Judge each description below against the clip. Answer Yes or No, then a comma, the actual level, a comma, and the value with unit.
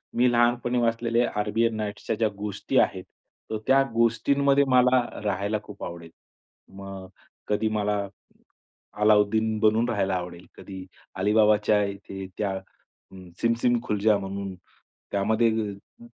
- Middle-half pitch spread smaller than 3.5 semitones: Yes, average, 2.7 semitones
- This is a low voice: Yes, low, 105 Hz